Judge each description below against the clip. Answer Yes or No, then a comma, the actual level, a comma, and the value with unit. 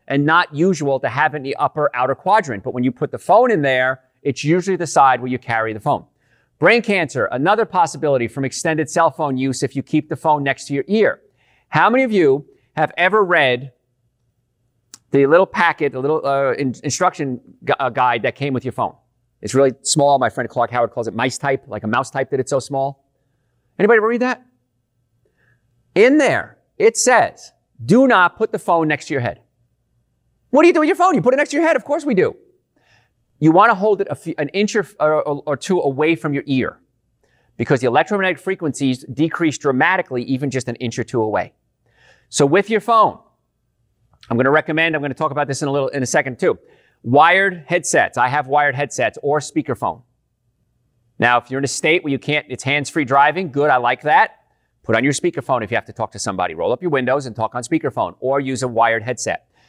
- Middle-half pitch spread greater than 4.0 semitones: Yes, average, 4.6 semitones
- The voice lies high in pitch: No, medium, 140 Hz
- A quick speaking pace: Yes, fast, 220 wpm